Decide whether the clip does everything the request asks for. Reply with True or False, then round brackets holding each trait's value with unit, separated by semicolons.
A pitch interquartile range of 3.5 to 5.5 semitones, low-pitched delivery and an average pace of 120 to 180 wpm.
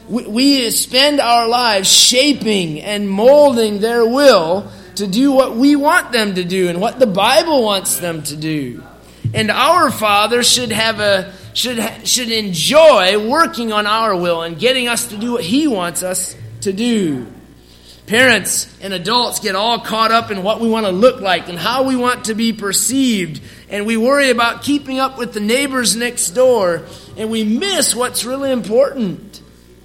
False (4.5 semitones; 225 Hz; 175 wpm)